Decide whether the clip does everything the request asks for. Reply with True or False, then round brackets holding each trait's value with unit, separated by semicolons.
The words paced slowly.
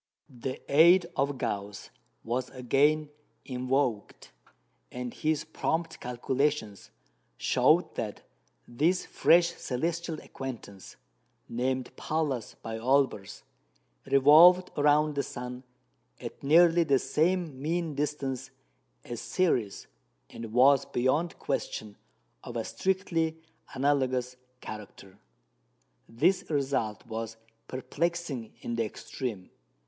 True (100 wpm)